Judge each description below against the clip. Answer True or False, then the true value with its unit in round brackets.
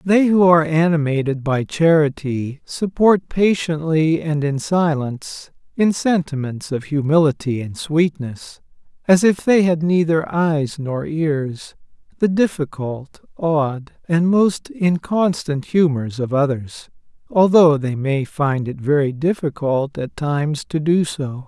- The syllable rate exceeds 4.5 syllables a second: False (3.8 syllables/s)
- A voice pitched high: False (155 Hz)